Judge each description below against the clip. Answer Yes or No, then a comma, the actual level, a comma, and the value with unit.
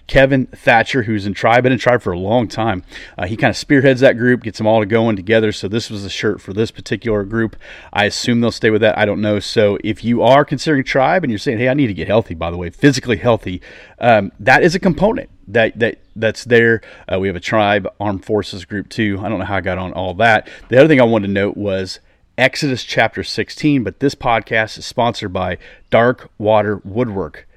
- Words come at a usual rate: No, fast, 240 wpm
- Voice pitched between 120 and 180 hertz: No, low, 110 Hz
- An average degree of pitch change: Yes, average, 3.7 semitones